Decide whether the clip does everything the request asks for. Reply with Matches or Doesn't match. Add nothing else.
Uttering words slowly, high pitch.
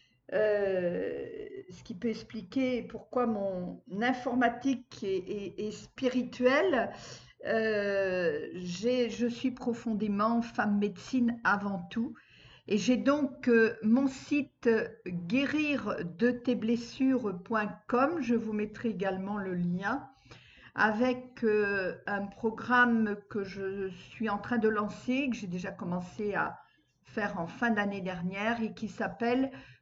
Matches